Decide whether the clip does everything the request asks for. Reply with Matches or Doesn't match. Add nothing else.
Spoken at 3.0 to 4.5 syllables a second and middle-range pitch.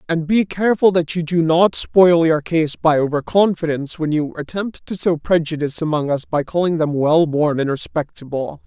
Doesn't match